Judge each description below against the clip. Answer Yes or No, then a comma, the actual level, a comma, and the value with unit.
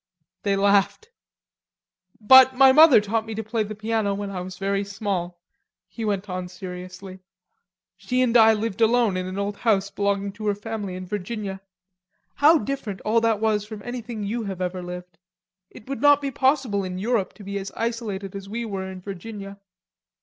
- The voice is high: Yes, high, 205 Hz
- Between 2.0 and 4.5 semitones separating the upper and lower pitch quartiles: Yes, average, 2.9 semitones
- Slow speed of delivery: No, average, 185 wpm